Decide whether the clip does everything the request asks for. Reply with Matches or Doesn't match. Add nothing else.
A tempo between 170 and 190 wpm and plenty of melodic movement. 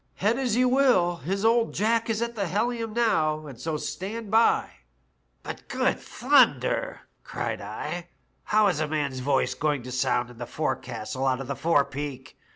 Matches